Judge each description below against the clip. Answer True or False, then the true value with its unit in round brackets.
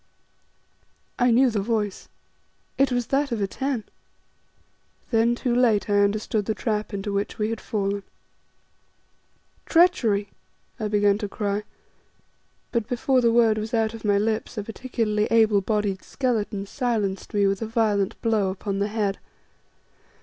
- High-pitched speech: True (215 Hz)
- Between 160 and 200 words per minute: False (145 wpm)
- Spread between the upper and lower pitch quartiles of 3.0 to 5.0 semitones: False (2.4 semitones)